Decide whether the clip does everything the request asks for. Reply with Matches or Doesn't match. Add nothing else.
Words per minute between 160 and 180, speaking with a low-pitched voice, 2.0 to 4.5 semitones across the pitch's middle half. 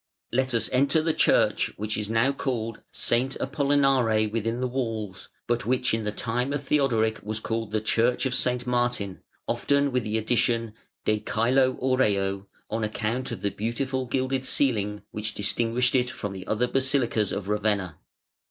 Matches